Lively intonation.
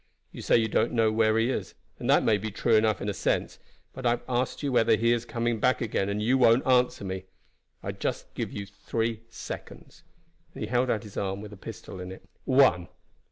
No: average, 2.8 semitones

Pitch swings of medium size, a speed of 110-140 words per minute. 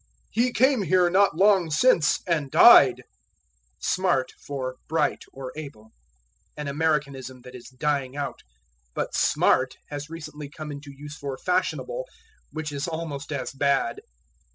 Yes: average, 3.7 semitones; slow, 135 wpm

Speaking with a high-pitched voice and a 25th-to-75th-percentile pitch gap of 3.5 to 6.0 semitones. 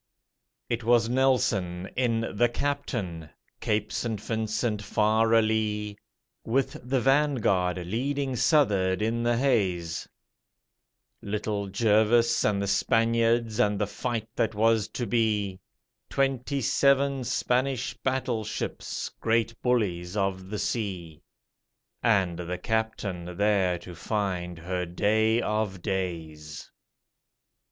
No: low, 110 Hz; average, 3.8 semitones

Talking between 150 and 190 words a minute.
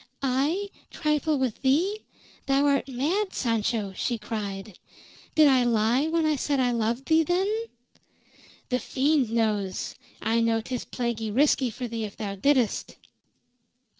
No: average, 140 wpm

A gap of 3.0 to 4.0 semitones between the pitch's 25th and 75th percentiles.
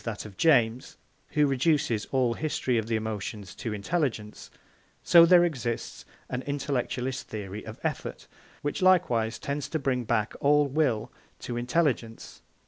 No: average, 4.7 semitones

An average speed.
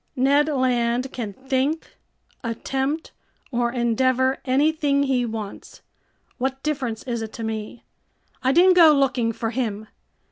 No: slow, 130 wpm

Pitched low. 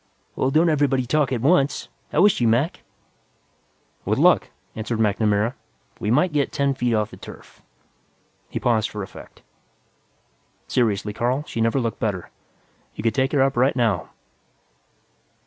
Yes: low, 120 Hz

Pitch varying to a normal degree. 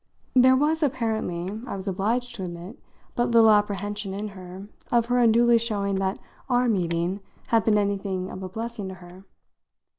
Yes: average, 3.7 semitones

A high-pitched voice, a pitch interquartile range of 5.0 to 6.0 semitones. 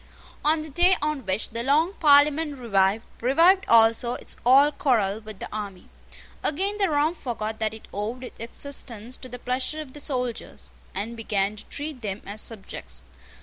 Yes: very high, 250 Hz; average, 5.3 semitones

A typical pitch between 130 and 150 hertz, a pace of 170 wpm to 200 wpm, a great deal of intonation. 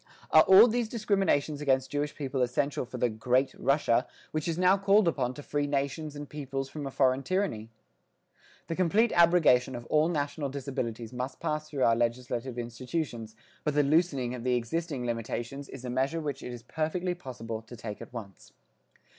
No: medium, 140 Hz; average, 180 wpm; average, 4.2 semitones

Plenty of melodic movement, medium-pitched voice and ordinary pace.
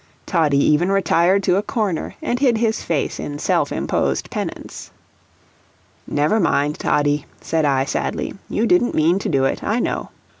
Yes: wide, 6.2 semitones; medium, 170 Hz; average, 160 wpm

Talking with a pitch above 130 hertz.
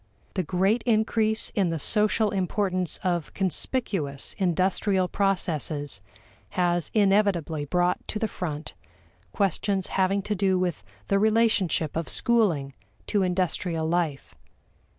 Yes: medium, 185 Hz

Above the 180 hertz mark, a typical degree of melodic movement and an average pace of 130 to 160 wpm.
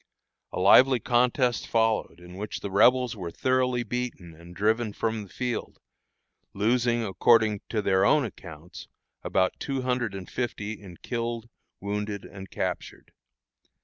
No: low, 110 Hz; average, 3.8 semitones; average, 140 wpm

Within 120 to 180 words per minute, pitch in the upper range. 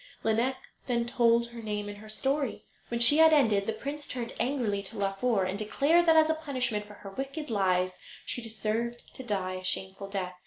No: average, 200 wpm; high, 230 Hz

